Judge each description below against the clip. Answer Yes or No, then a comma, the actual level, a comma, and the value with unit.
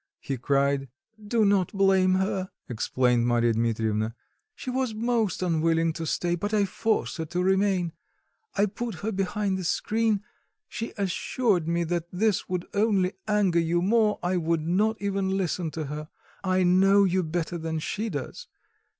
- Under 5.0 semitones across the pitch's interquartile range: Yes, average, 3.9 semitones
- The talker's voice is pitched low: No, medium, 185 Hz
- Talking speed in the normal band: Yes, average, 160 wpm